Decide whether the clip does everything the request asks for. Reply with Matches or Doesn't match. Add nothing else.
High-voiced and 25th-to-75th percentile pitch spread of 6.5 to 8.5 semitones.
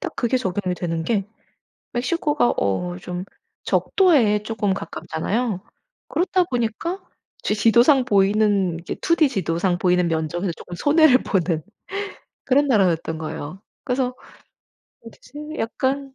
Matches